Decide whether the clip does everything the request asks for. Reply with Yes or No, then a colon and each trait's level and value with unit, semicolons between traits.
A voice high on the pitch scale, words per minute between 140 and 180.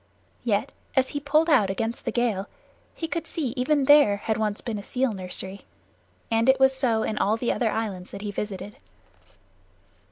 No: high, 225 Hz; average, 190 wpm